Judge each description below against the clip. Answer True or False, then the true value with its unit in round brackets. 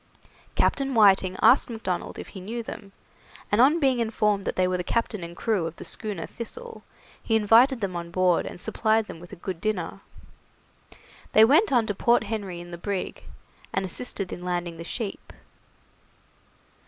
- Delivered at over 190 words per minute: False (180 wpm)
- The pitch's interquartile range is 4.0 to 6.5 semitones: True (4.3 semitones)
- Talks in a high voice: True (205 Hz)